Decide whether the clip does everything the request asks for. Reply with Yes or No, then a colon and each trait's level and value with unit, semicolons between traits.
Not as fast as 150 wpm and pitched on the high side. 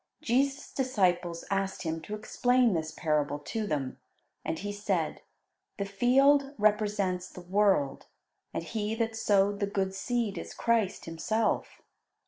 Yes: average, 140 wpm; high, 205 Hz